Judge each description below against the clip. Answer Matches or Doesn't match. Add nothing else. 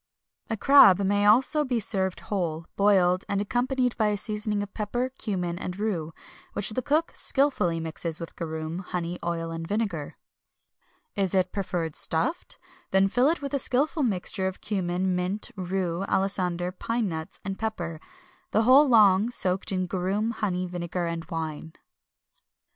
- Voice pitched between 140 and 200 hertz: Matches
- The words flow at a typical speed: Matches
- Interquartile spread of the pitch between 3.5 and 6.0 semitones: Matches